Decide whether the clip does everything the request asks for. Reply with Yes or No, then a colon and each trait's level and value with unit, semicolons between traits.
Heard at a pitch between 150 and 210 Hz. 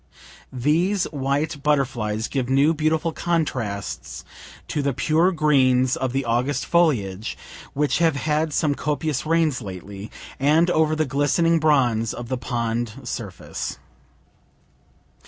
No: medium, 140 Hz